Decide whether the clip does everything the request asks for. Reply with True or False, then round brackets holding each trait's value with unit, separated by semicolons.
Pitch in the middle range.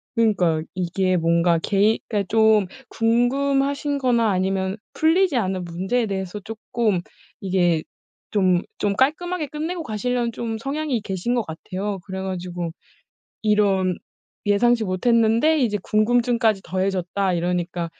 False (210 Hz)